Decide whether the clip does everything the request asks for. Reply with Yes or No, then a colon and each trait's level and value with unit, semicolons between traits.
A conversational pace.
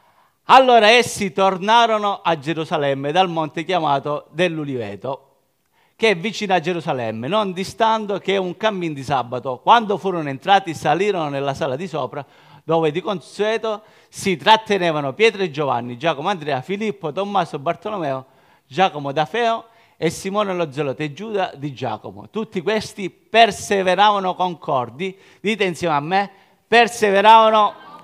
Yes: average, 135 wpm